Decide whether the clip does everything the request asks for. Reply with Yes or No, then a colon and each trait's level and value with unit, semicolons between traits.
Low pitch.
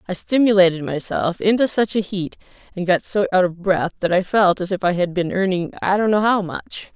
No: high, 190 Hz